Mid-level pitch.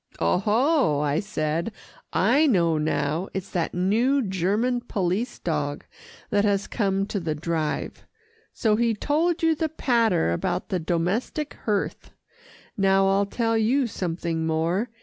No: high, 195 Hz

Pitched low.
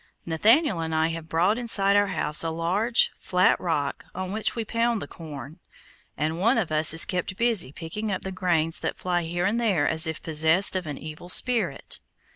No: medium, 175 Hz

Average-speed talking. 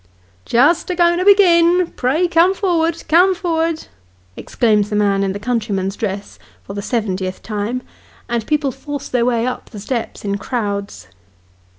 Yes: average, 165 wpm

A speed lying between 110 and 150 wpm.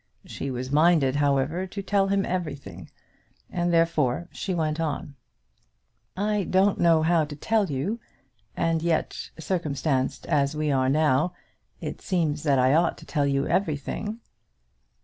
Yes: average, 145 wpm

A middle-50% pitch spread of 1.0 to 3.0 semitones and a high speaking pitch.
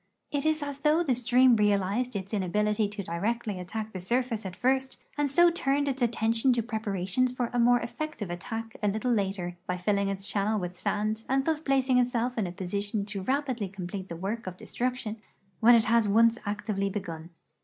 No: average, 4.2 semitones; high, 220 Hz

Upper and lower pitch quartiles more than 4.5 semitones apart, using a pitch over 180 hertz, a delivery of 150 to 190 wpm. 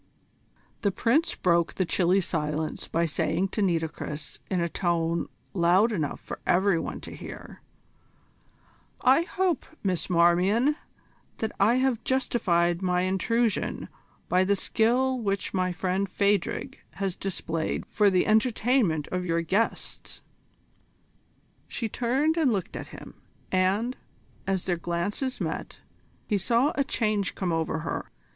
No: average, 4.9 semitones; high, 190 Hz; slow, 135 wpm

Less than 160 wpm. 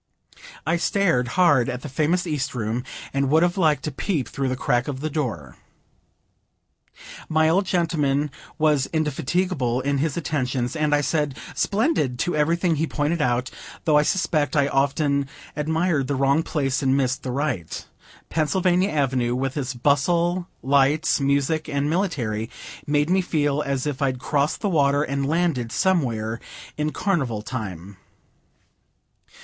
Yes: average, 150 wpm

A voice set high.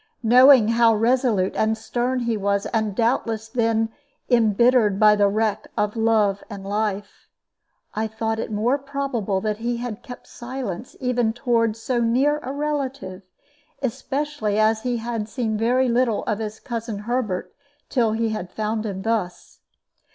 Yes: high, 225 Hz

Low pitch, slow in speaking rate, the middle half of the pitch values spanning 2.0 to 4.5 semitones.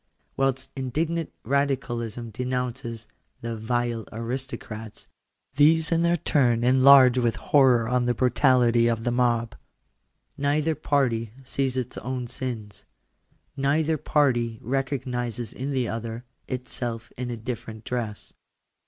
Yes: low, 125 Hz; slow, 120 wpm; narrow, 2.6 semitones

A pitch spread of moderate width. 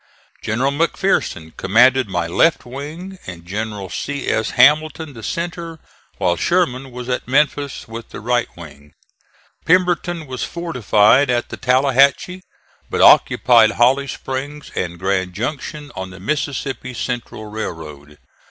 No: wide, 5.9 semitones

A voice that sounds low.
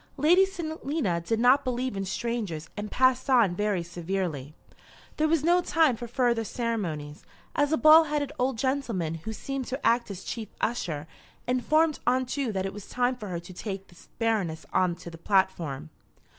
No: high, 230 Hz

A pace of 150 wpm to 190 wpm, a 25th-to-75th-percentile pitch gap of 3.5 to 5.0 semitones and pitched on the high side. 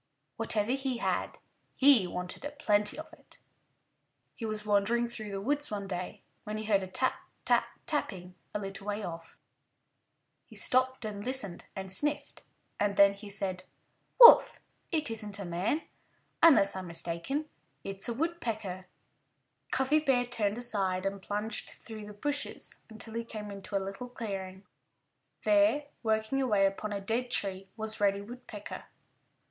Yes: average, 155 wpm; average, 4.2 semitones; high, 210 Hz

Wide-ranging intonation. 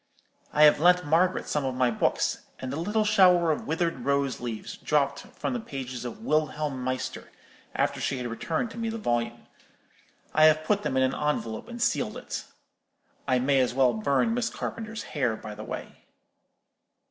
Yes: wide, 5.8 semitones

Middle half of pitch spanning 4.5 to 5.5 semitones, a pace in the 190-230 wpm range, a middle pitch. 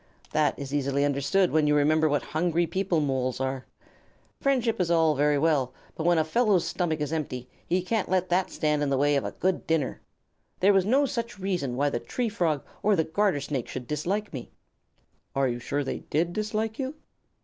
Yes: average, 5.0 semitones; fast, 205 wpm; medium, 160 Hz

